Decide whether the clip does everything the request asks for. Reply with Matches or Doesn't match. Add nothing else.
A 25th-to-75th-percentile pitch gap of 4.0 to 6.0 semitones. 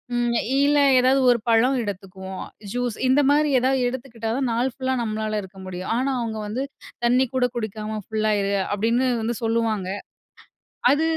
Doesn't match